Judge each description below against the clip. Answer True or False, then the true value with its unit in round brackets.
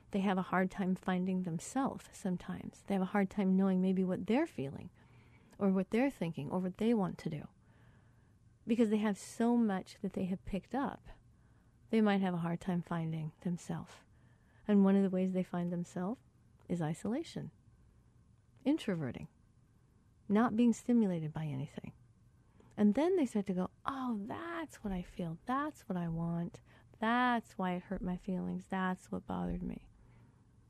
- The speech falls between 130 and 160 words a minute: False (170 wpm)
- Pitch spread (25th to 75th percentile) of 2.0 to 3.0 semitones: False (4.0 semitones)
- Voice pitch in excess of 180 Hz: True (190 Hz)